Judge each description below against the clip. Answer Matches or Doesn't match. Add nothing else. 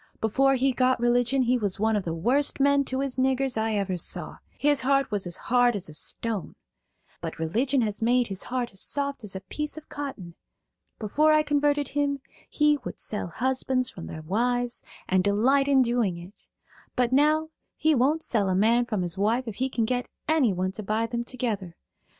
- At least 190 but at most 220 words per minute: Matches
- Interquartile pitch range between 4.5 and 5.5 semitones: Matches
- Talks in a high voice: Matches